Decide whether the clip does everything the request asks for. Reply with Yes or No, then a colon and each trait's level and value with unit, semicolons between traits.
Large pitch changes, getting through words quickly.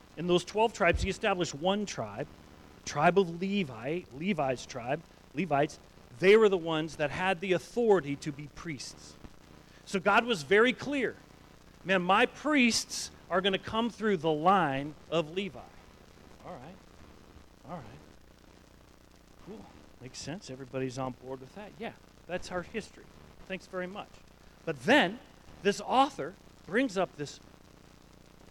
No: wide, 5.7 semitones; average, 145 wpm